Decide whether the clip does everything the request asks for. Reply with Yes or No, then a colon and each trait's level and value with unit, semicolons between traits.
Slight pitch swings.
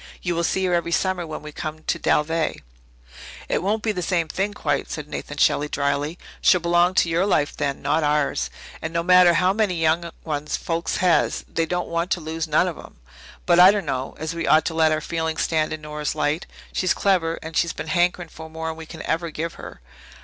Yes: narrow, 2.1 semitones